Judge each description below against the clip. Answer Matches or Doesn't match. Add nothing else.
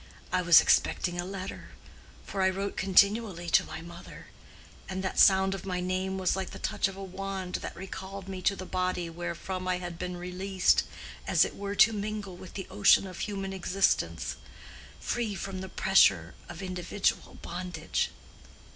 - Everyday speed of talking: Matches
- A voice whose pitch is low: Doesn't match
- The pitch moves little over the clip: Matches